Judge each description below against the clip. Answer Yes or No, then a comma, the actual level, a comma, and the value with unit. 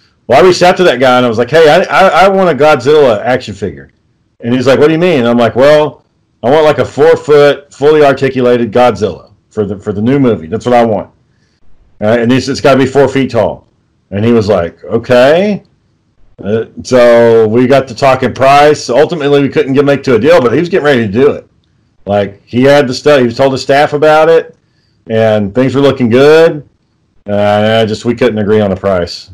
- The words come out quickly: Yes, fast, 235 wpm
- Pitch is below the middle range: Yes, low, 125 Hz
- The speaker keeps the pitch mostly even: No, average, 4.4 semitones